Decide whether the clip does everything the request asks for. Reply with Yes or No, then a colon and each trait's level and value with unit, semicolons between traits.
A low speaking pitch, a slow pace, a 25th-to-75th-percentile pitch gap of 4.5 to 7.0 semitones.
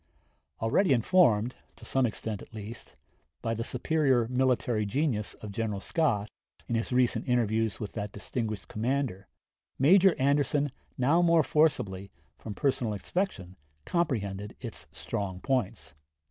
Yes: low, 120 Hz; slow, 130 wpm; average, 5.1 semitones